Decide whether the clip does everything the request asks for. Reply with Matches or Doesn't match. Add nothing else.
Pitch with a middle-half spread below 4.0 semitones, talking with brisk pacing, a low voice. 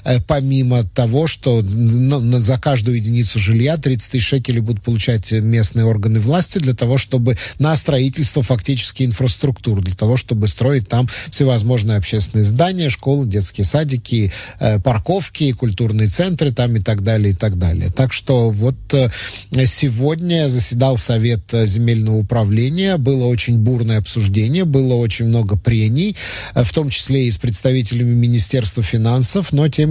Doesn't match